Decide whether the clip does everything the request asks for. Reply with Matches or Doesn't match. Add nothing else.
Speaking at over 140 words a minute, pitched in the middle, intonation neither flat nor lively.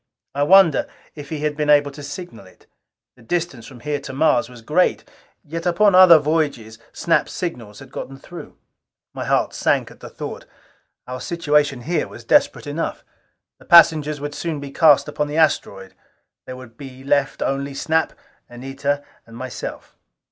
Matches